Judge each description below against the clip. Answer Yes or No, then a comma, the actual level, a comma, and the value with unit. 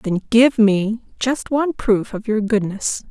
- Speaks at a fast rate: No, average, 175 wpm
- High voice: Yes, high, 220 Hz